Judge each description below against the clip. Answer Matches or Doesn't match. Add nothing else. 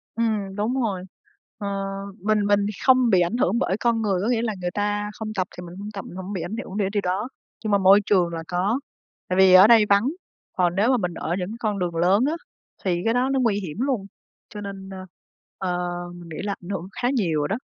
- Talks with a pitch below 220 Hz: Matches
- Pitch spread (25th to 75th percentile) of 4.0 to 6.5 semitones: Doesn't match